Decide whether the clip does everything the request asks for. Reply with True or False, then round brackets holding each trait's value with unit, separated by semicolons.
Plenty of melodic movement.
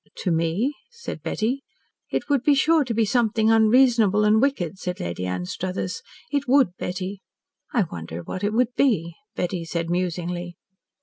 True (6.0 semitones)